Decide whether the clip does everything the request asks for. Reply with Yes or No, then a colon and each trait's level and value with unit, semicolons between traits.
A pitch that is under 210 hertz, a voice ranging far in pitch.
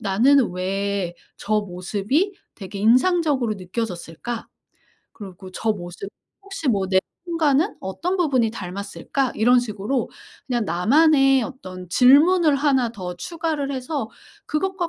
No: high, 235 Hz; wide, 6.7 semitones